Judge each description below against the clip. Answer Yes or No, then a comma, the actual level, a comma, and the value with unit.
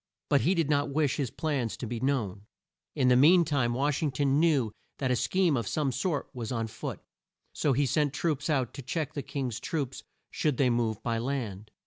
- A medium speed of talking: No, fast, 210 wpm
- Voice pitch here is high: No, low, 135 Hz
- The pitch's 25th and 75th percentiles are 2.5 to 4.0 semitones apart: Yes, average, 3.7 semitones